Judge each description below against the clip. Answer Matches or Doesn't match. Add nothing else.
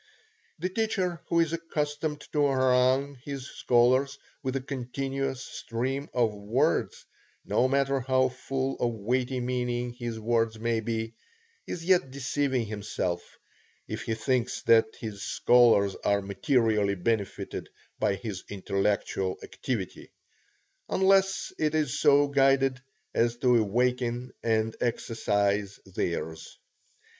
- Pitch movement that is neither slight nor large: Matches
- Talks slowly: Matches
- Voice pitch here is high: Doesn't match